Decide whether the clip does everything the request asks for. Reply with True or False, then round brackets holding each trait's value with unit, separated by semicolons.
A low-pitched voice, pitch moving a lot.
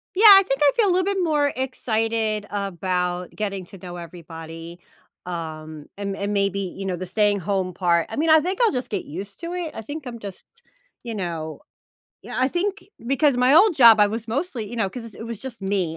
False (210 Hz; 6.7 semitones)